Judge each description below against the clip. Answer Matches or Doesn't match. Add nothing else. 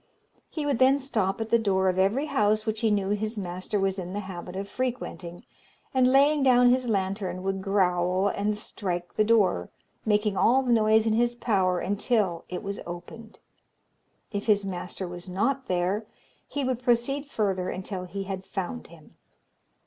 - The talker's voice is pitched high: Matches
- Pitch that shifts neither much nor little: Matches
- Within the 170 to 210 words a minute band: Matches